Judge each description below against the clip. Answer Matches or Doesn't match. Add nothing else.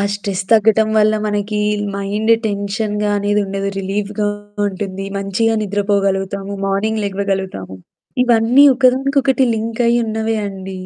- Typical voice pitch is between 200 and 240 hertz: Matches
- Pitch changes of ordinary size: Doesn't match